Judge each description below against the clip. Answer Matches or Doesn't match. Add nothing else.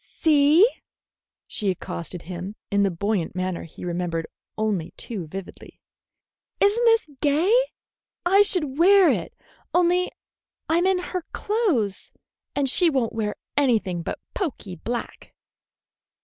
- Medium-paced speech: Doesn't match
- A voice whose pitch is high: Matches